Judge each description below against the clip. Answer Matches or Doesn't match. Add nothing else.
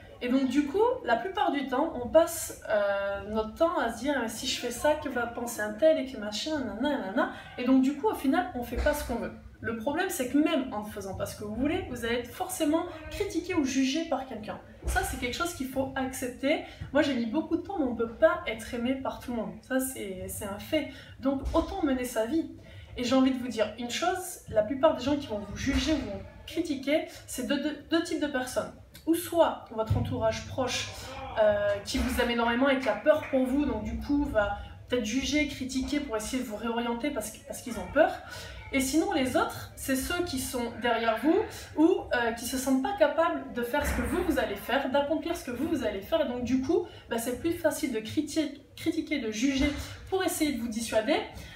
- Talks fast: Matches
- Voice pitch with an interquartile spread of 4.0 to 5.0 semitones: Matches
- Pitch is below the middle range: Doesn't match